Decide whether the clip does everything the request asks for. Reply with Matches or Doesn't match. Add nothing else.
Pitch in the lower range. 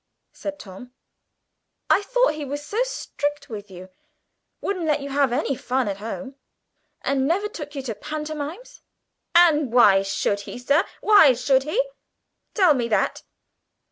Doesn't match